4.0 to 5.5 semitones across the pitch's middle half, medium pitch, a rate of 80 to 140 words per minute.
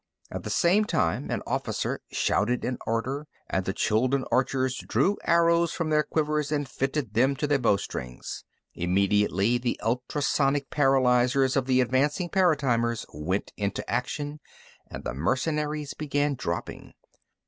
No: average, 4.3 semitones; low, 130 Hz; slow, 135 wpm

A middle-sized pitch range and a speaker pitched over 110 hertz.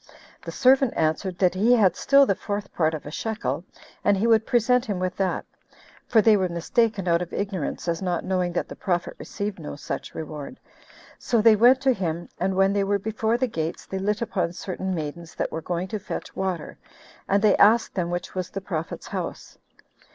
Yes: average, 4.0 semitones; high, 190 Hz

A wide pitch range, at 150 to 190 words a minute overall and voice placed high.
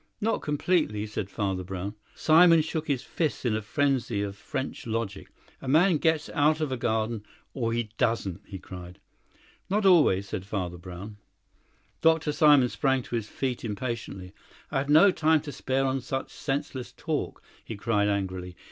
No: wide, 6.7 semitones; average, 165 wpm; low, 120 Hz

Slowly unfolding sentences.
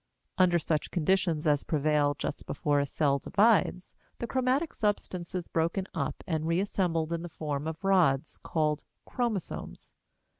No: average, 145 wpm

